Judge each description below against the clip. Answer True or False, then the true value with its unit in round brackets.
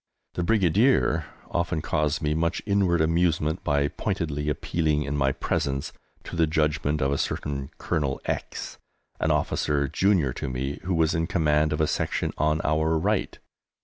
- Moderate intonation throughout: False (2.3 semitones)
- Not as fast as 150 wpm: False (160 wpm)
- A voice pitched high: False (75 Hz)